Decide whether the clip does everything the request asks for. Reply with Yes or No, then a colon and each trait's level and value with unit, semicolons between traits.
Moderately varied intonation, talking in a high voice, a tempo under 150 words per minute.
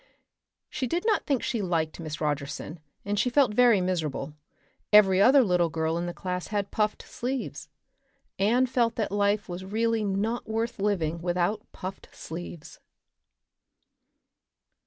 Yes: average, 4.8 semitones; high, 200 Hz; average, 140 wpm